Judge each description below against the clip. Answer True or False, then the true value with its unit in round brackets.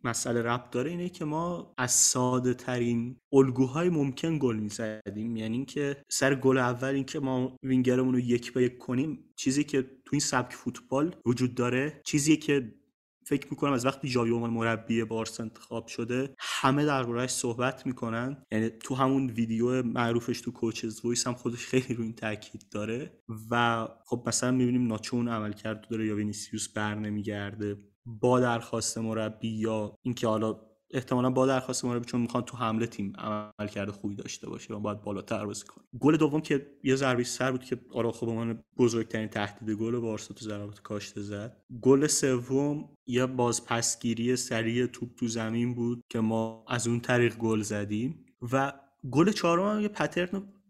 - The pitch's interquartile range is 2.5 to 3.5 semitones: True (2.8 semitones)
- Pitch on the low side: True (120 Hz)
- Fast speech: True (170 wpm)